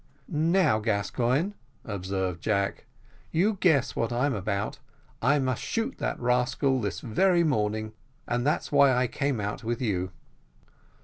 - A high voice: No, low, 125 Hz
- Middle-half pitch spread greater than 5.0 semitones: Yes, wide, 5.4 semitones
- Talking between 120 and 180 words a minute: Yes, slow, 135 wpm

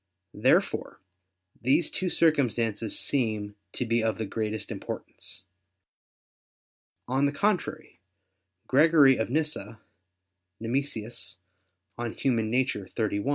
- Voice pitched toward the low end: Yes, low, 120 Hz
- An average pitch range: Yes, average, 4.4 semitones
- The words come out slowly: Yes, slow, 100 wpm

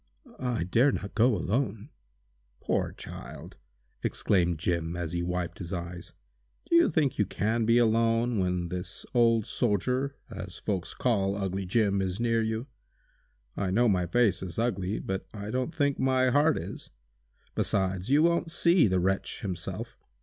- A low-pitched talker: Yes, low, 105 Hz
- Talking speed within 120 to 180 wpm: Yes, average, 155 wpm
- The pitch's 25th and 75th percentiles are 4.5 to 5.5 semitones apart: Yes, average, 4.9 semitones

